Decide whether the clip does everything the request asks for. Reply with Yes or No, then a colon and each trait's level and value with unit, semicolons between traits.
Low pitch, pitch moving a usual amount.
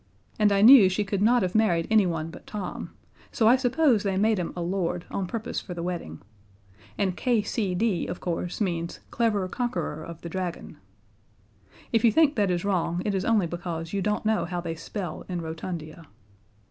No: high, 190 Hz; average, 4.0 semitones